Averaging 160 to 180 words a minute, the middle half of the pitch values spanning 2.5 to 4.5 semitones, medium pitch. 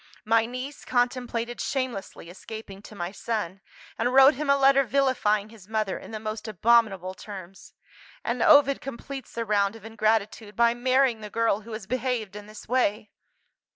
No: average, 165 wpm; average, 3.4 semitones; high, 225 Hz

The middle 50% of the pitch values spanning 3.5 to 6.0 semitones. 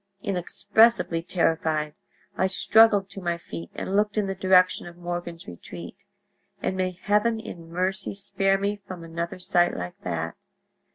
No: average, 2.9 semitones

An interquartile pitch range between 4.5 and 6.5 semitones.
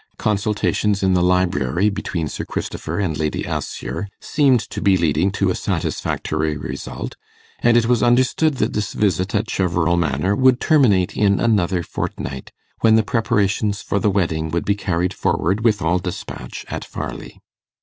No: average, 3.9 semitones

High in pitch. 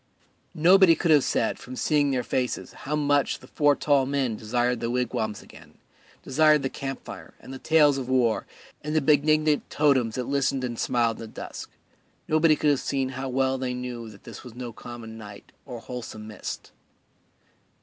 No: low, 130 Hz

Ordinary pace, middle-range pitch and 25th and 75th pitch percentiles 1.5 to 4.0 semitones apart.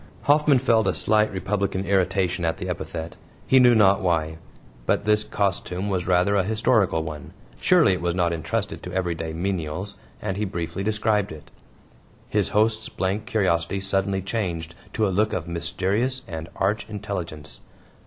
No: average, 160 wpm; very low, 95 Hz; average, 3.7 semitones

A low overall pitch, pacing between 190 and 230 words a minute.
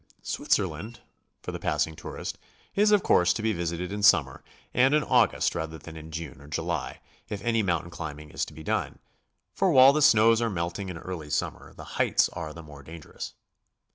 Yes: very low, 85 Hz; average, 195 wpm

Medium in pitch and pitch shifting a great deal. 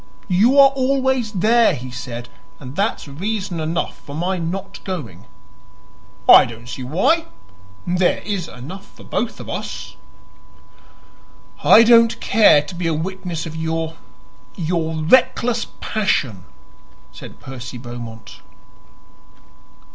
Yes: medium, 175 Hz; wide, 7.2 semitones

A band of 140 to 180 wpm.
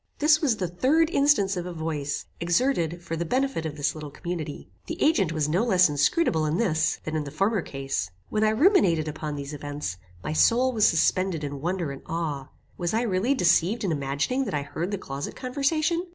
No: fast, 205 wpm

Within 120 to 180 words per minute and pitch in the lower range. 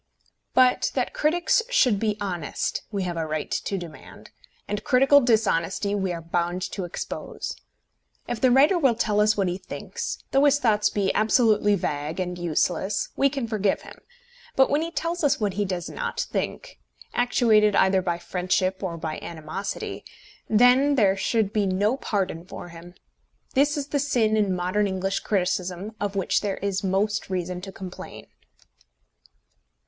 No: average, 165 wpm; high, 200 Hz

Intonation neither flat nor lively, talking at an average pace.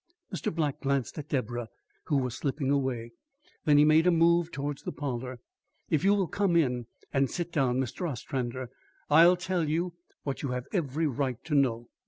Yes: average, 4.4 semitones; average, 185 wpm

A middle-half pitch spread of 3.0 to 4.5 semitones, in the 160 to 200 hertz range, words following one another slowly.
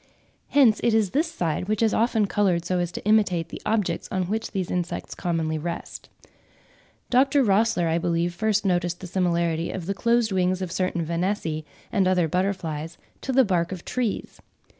No: average, 4.0 semitones; medium, 185 Hz; average, 180 wpm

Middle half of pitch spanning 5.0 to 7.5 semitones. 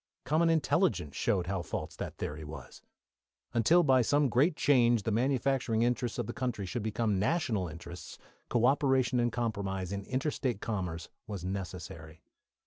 Yes: average, 5.3 semitones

